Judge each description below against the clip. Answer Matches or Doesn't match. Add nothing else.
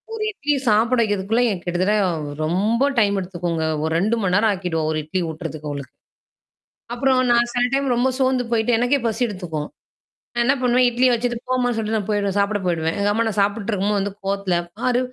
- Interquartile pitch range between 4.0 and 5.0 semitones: Matches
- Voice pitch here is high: Matches